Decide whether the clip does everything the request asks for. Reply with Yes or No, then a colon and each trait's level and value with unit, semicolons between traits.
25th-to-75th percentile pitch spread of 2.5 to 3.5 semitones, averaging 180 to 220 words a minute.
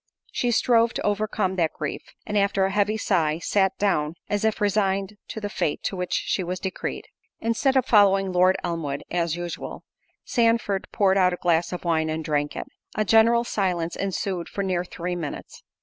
Yes: average, 3.2 semitones; average, 185 wpm